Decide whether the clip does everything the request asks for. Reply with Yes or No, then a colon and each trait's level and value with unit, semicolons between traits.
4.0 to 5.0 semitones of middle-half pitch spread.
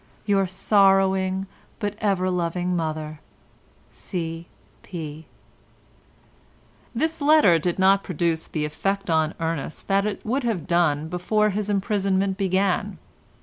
No: average, 3.1 semitones